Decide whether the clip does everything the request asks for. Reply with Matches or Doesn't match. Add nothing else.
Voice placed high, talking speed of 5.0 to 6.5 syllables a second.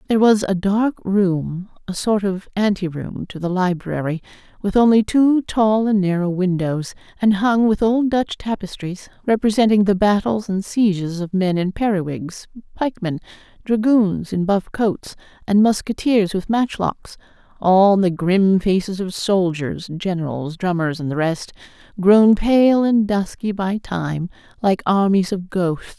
Doesn't match